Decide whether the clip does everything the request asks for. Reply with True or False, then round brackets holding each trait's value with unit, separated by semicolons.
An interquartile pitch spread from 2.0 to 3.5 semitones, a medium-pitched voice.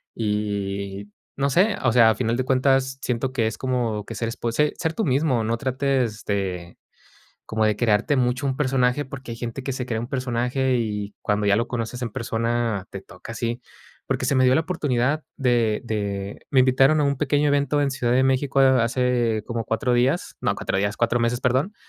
False (3.1 semitones; 125 Hz)